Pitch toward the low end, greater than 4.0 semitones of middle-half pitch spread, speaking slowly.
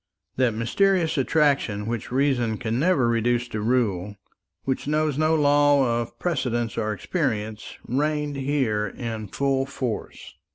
Yes: low, 125 Hz; average, 4.4 semitones; slow, 130 wpm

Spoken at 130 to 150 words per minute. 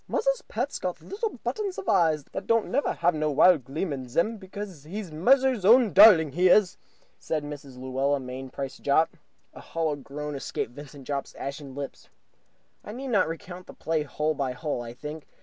No: average, 185 wpm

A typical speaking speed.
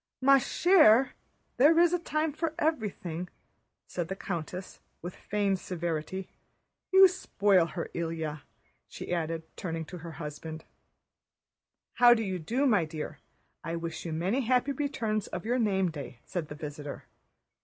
Yes: average, 145 wpm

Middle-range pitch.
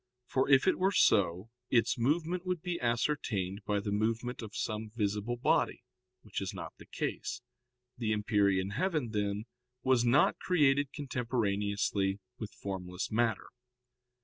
No: low, 115 Hz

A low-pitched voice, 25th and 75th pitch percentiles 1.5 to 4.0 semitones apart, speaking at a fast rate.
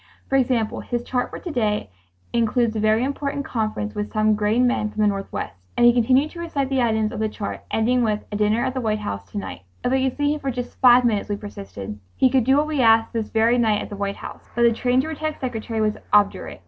No: high, 230 Hz; average, 3.3 semitones; fast, 255 wpm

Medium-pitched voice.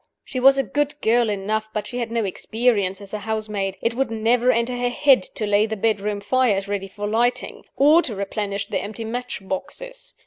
No: high, 220 Hz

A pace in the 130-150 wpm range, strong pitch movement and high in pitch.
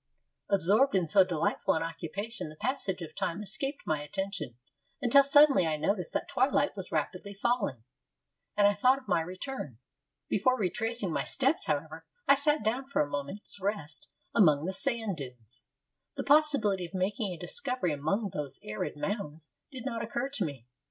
No: average, 170 wpm; wide, 7.3 semitones; high, 195 Hz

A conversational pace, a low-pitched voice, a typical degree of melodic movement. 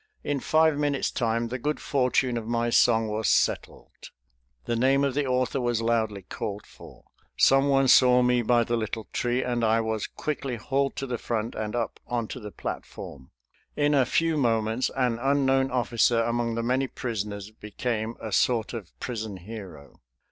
Yes: average, 170 wpm; low, 120 Hz; average, 3.0 semitones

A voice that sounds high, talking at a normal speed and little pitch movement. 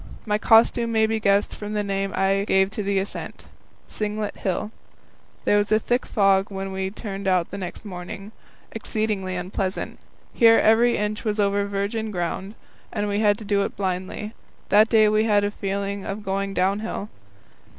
Yes: high, 205 Hz; average, 170 wpm; narrow, 1.7 semitones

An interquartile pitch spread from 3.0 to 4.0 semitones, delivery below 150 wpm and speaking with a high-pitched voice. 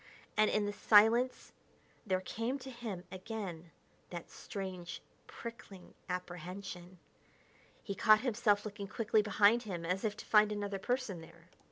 Yes: average, 3.3 semitones; average, 140 wpm; high, 205 Hz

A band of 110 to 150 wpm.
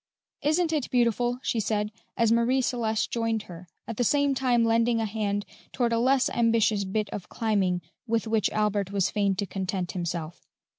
No: average, 180 wpm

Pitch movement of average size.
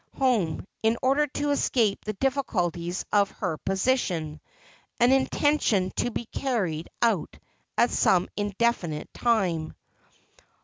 No: wide, 6.3 semitones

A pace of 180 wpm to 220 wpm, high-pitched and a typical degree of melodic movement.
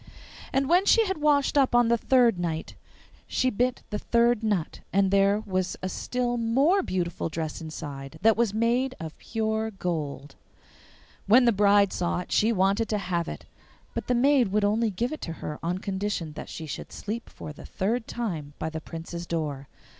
No: average, 185 wpm; high, 205 Hz; wide, 5.8 semitones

